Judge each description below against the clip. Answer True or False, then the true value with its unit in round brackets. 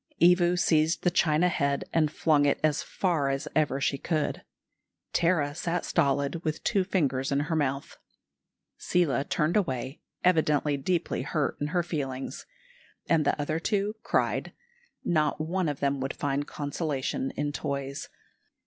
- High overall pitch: False (150 Hz)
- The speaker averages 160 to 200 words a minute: False (150 wpm)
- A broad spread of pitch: False (3.4 semitones)